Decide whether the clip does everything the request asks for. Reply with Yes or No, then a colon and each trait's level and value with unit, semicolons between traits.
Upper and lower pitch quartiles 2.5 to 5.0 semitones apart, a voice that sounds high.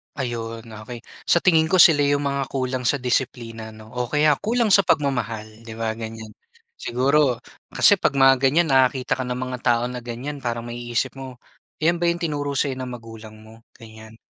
No: average, 3.7 semitones; low, 125 Hz